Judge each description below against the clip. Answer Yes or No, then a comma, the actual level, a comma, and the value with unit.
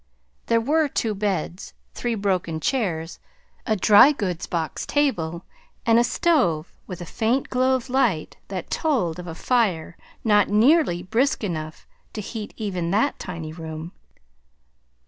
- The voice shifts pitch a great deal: Yes, wide, 6.4 semitones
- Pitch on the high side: Yes, high, 205 Hz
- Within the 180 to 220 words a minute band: No, average, 145 wpm